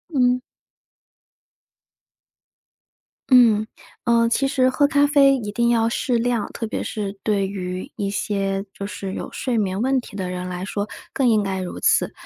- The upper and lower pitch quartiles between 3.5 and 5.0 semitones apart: Yes, average, 4.1 semitones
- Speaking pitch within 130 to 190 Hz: No, high, 215 Hz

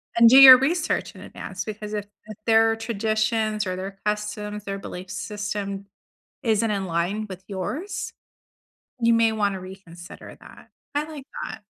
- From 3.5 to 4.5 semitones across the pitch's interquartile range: No, narrow, 2.5 semitones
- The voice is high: Yes, high, 210 Hz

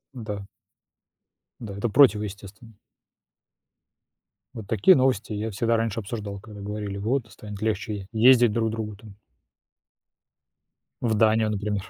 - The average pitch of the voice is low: Yes, low, 110 Hz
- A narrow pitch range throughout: Yes, narrow, 1.9 semitones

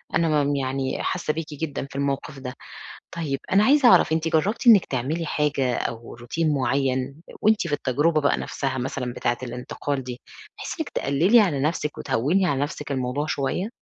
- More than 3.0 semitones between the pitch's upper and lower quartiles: Yes, average, 3.6 semitones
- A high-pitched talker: No, medium, 145 Hz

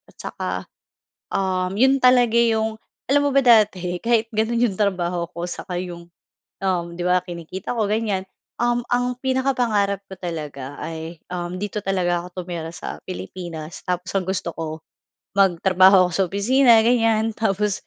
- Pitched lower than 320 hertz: Yes, high, 190 Hz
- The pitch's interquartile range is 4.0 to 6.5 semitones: Yes, average, 4.3 semitones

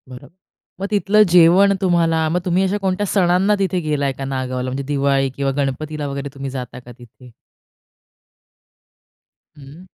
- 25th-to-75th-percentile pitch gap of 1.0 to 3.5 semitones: No, average, 5.2 semitones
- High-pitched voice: No, medium, 150 Hz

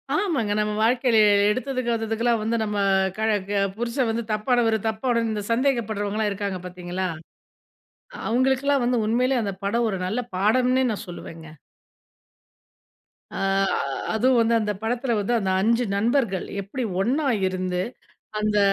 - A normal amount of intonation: Yes, average, 3.2 semitones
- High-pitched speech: Yes, high, 225 Hz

